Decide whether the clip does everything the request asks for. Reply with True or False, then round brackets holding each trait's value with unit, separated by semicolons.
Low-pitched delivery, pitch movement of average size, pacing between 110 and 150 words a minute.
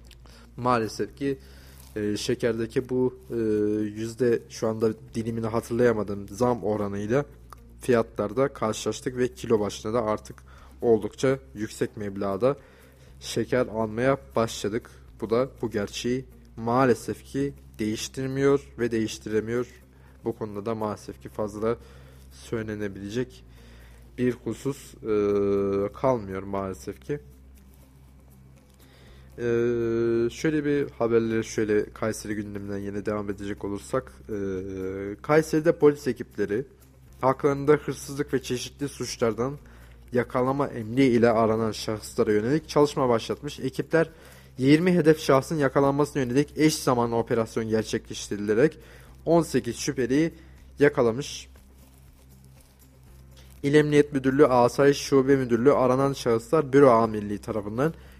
False (115 Hz; 4.8 semitones; 100 wpm)